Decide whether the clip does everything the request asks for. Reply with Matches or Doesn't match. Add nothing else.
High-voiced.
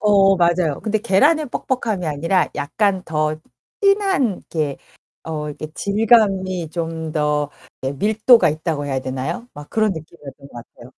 Doesn't match